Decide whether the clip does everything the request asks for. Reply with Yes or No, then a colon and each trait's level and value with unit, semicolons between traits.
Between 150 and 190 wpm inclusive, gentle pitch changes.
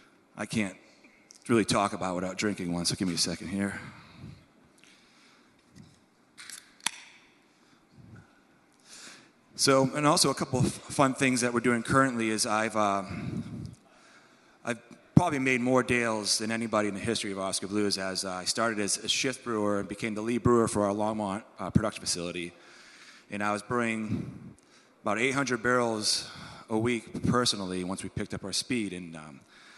No: average, 160 wpm; average, 3.9 semitones